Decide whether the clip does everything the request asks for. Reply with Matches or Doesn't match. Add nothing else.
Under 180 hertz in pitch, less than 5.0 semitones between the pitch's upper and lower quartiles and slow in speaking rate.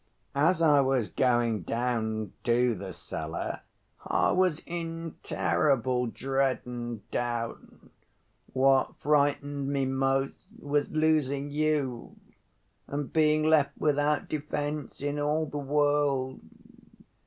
Matches